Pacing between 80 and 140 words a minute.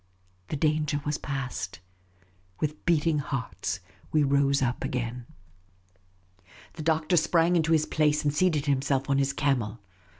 Yes: slow, 135 wpm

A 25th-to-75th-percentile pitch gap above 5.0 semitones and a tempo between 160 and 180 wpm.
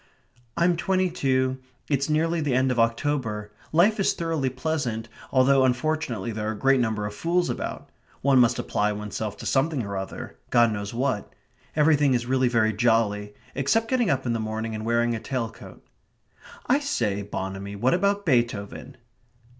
Yes: wide, 5.5 semitones; average, 170 wpm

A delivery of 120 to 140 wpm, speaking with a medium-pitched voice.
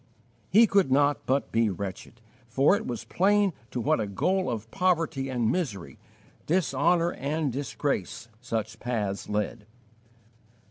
No: slow, 135 wpm; low, 130 Hz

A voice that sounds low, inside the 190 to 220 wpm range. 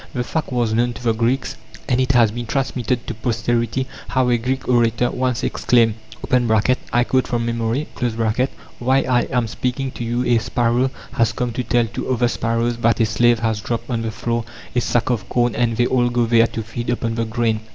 Yes: low, 120 Hz; fast, 205 wpm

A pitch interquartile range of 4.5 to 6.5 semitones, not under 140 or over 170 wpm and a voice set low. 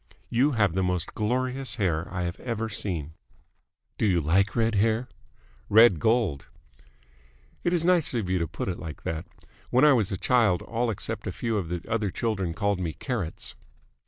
No: average, 4.8 semitones; average, 185 wpm; low, 105 Hz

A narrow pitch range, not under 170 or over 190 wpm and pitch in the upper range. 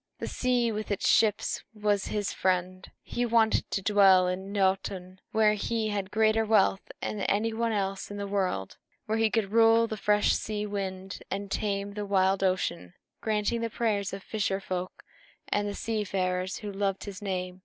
Yes: narrow, 2.2 semitones; average, 180 wpm; high, 200 Hz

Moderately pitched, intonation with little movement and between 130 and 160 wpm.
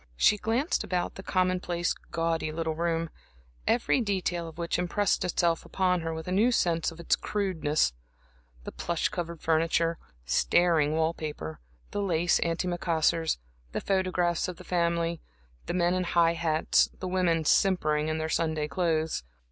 Yes: medium, 170 Hz; narrow, 2.1 semitones; average, 155 wpm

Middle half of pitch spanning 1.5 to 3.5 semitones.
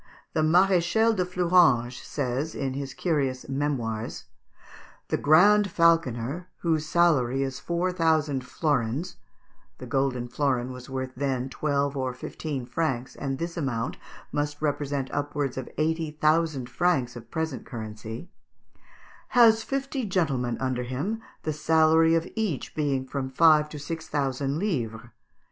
No: average, 4.2 semitones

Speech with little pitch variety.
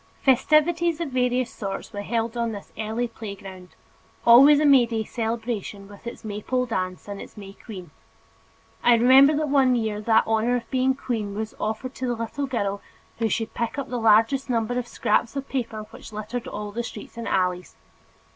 No: average, 3.3 semitones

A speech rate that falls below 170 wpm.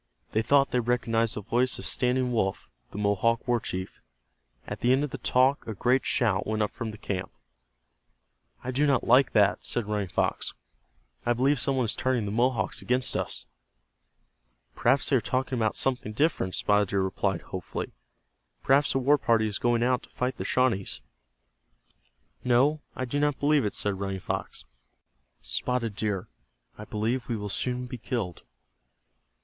No: average, 175 wpm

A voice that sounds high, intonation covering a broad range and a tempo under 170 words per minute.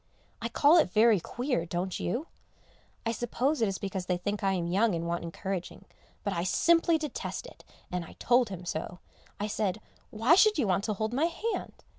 No: high, 210 Hz; wide, 5.9 semitones; average, 200 wpm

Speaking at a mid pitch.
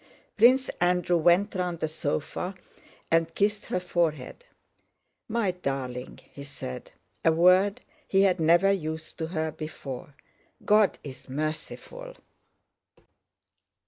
Yes: medium, 175 Hz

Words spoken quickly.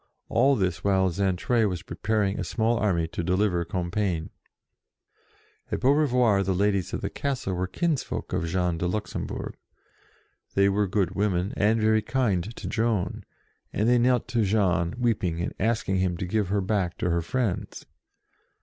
No: average, 165 wpm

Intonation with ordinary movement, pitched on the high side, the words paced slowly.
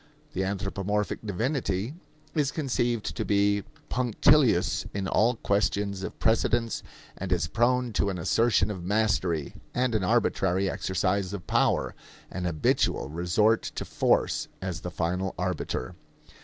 No: average, 3.8 semitones; low, 100 Hz; slow, 130 wpm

